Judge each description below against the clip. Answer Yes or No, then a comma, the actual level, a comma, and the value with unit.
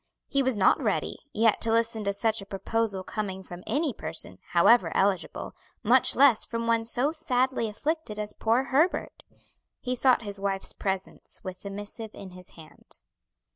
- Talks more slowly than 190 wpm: Yes, average, 170 wpm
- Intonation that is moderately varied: Yes, average, 4.1 semitones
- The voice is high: Yes, high, 220 Hz